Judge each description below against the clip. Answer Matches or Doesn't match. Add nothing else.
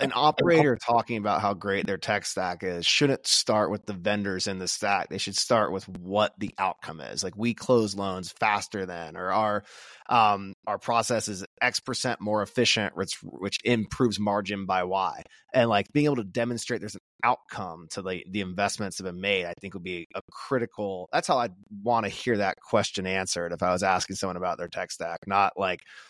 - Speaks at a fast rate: Matches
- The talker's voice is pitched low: Matches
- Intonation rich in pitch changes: Doesn't match